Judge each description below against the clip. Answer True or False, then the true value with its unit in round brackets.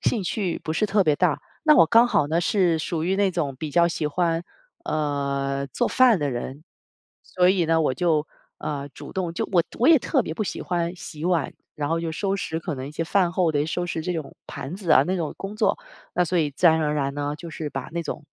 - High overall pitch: False (165 Hz)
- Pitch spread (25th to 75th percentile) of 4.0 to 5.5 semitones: False (3.4 semitones)